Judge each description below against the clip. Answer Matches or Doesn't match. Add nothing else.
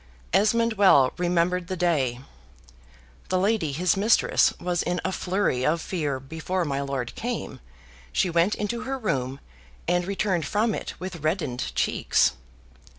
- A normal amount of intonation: Matches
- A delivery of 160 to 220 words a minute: Doesn't match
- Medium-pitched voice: Matches